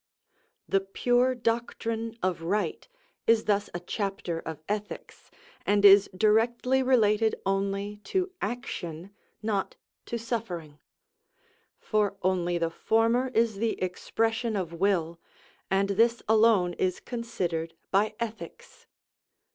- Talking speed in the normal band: No, slow, 115 wpm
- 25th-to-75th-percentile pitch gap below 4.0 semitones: Yes, average, 3.6 semitones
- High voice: Yes, high, 205 Hz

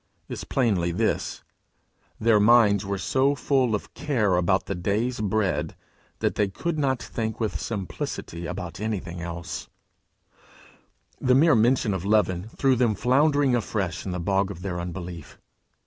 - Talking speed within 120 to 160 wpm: Yes, average, 145 wpm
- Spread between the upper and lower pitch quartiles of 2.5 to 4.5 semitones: No, average, 5.1 semitones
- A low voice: Yes, low, 105 Hz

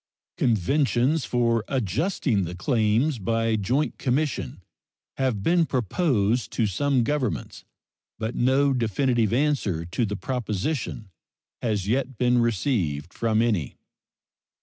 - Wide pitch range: No, average, 4.3 semitones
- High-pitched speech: No, low, 120 Hz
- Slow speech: Yes, slow, 110 wpm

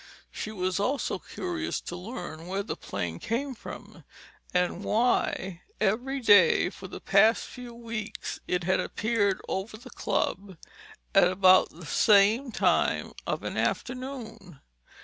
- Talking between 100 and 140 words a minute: Yes, slow, 135 wpm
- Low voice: No, high, 205 Hz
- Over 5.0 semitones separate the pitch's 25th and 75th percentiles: No, average, 4.3 semitones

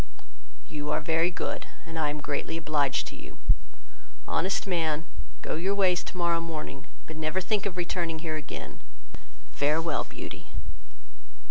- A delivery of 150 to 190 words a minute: No, average, 140 wpm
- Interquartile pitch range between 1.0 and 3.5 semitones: Yes, narrow, 2.5 semitones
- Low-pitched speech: No, medium, 165 Hz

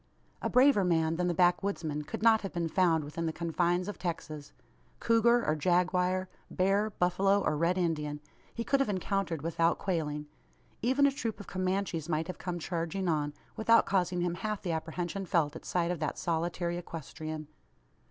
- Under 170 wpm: No, average, 175 wpm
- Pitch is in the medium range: Yes, medium, 175 Hz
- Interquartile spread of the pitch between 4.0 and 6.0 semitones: No, average, 3.2 semitones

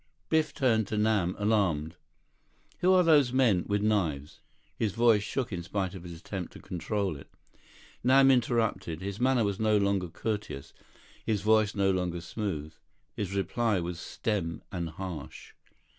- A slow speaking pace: No, average, 150 wpm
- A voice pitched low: Yes, low, 100 Hz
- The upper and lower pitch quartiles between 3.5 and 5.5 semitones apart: Yes, average, 4.0 semitones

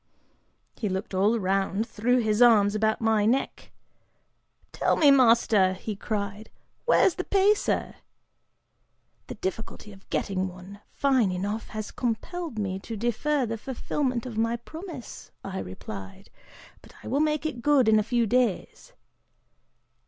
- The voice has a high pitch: Yes, high, 225 Hz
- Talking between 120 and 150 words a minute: Yes, average, 140 wpm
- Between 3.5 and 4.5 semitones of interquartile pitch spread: Yes, average, 4.0 semitones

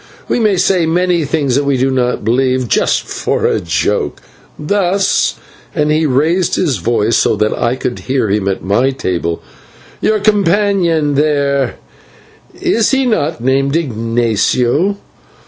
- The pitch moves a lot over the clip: Yes, wide, 6.3 semitones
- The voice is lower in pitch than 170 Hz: Yes, medium, 140 Hz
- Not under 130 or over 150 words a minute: Yes, average, 140 wpm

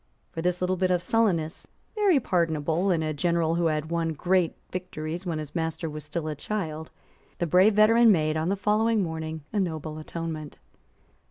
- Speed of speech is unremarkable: Yes, average, 180 wpm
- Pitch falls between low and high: Yes, medium, 170 Hz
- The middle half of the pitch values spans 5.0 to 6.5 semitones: No, average, 2.9 semitones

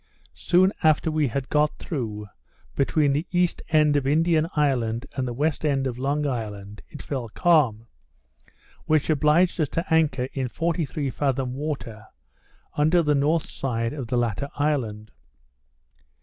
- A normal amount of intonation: Yes, average, 3.9 semitones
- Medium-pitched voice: Yes, medium, 145 Hz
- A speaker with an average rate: Yes, average, 150 wpm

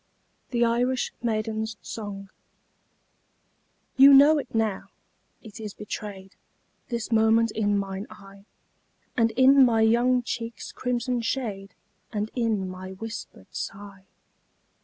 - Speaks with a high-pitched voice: Yes, high, 220 Hz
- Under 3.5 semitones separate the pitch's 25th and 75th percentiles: Yes, average, 2.9 semitones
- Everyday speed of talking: No, slow, 115 wpm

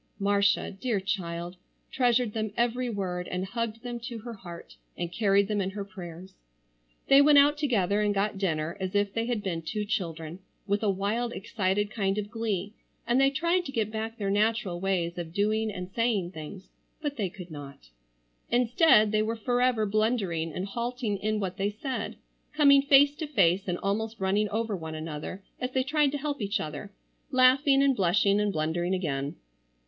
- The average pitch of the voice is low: No, high, 205 Hz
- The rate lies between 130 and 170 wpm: No, average, 185 wpm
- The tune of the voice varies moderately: Yes, average, 4.2 semitones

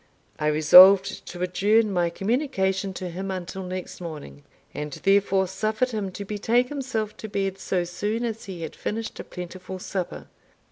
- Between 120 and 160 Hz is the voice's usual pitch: No, high, 195 Hz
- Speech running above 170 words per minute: No, average, 160 wpm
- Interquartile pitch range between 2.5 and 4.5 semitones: Yes, average, 3.0 semitones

